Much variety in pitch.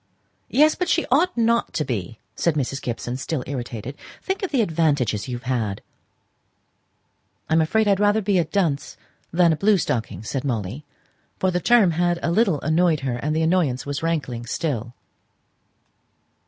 Yes: wide, 7.0 semitones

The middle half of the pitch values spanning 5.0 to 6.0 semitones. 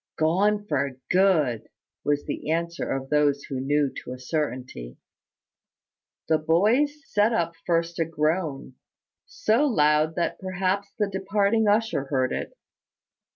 Yes: wide, 5.6 semitones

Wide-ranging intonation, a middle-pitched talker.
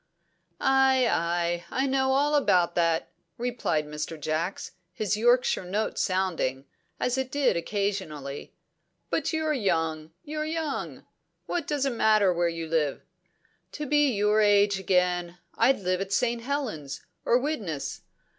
No: wide, 7.7 semitones; high, 200 Hz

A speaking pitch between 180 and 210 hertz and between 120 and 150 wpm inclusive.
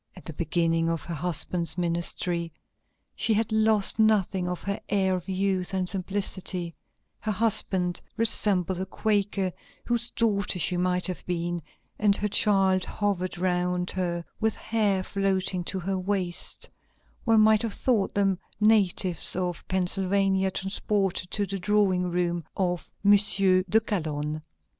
Yes: high, 190 Hz; average, 140 wpm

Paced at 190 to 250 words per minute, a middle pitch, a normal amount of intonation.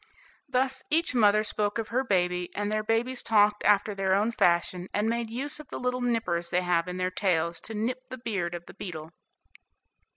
No: average, 200 wpm; high, 210 Hz; average, 4.7 semitones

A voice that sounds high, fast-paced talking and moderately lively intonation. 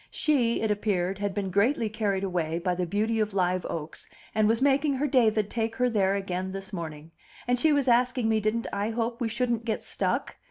Yes: high, 215 Hz; fast, 210 wpm; average, 3.6 semitones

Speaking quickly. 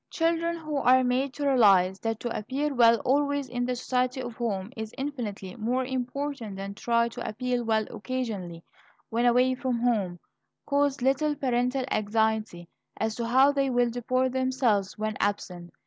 No: average, 165 wpm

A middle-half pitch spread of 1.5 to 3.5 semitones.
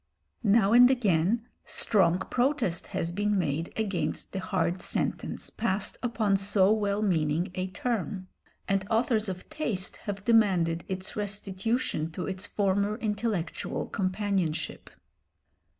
Yes: average, 2.8 semitones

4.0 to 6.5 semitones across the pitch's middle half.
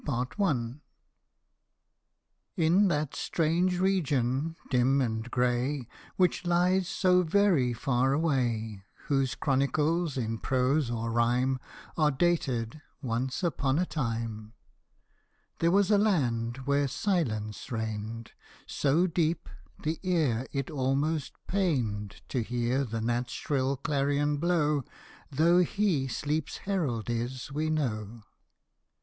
Yes: wide, 5.4 semitones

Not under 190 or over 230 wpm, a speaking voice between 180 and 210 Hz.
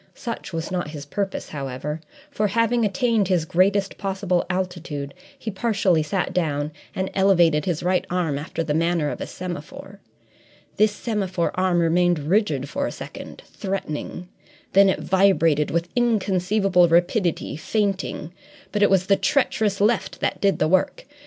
No: average, 150 wpm; medium, 185 Hz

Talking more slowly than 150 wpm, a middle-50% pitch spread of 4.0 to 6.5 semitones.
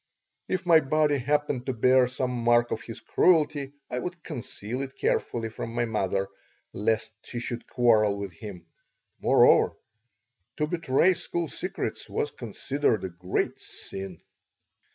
Yes: average, 140 wpm; average, 4.8 semitones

